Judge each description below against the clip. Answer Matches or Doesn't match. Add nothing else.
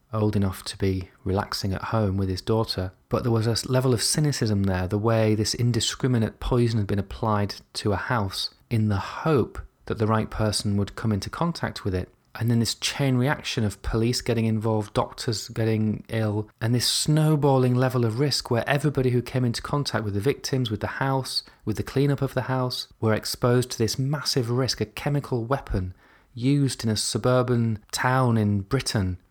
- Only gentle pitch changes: Doesn't match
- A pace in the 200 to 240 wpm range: Doesn't match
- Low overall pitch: Matches